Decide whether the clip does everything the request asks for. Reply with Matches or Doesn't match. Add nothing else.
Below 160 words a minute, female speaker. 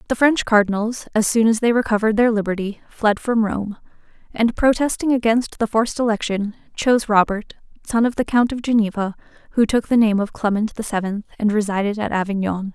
Doesn't match